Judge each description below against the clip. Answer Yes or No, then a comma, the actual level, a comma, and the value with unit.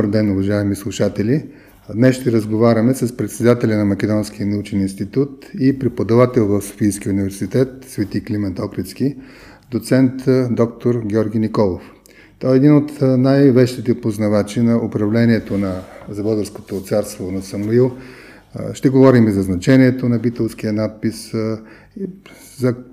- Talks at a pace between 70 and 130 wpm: Yes, average, 125 wpm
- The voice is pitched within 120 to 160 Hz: No, low, 110 Hz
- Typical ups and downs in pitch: Yes, average, 3.6 semitones